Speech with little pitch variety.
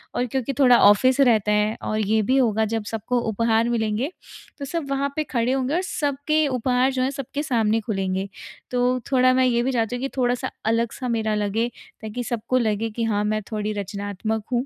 No: average, 3.2 semitones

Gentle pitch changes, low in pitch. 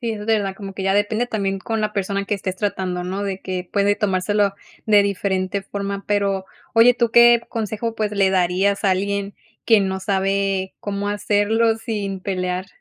No: narrow, 1.7 semitones; high, 200 Hz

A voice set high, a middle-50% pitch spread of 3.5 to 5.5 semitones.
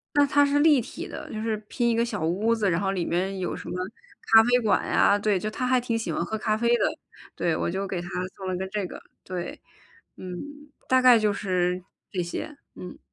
Yes: high, 210 Hz; average, 4.4 semitones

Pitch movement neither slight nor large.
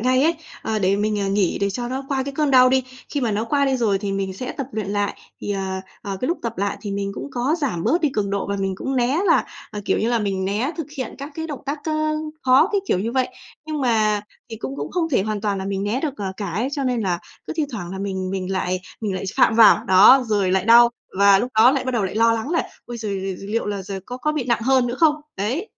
Yes: average, 4.8 semitones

